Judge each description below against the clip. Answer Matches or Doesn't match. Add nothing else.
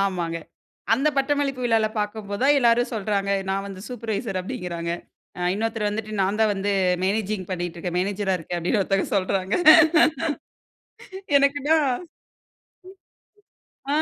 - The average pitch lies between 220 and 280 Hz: Doesn't match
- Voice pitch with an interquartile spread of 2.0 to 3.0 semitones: Doesn't match